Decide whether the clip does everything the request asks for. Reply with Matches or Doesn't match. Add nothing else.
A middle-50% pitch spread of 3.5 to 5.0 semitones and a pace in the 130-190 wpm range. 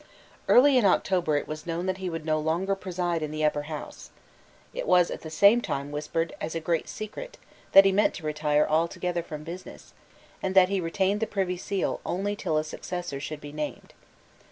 Doesn't match